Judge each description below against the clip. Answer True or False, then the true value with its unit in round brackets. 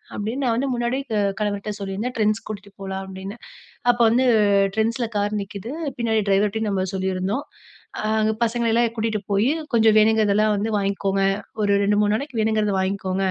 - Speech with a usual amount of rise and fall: False (2.3 semitones)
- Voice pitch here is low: False (210 Hz)